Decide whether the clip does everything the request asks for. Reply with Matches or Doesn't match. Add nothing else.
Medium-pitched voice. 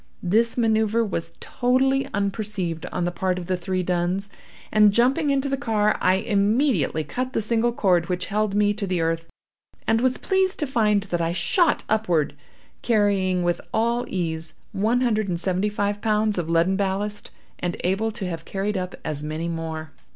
Doesn't match